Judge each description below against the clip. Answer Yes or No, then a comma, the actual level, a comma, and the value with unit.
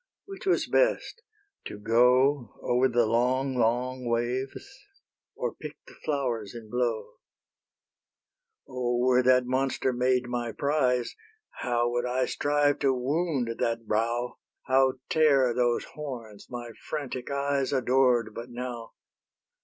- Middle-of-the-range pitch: No, low, 125 Hz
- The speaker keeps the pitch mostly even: Yes, narrow, 2.0 semitones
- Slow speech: Yes, slow, 125 wpm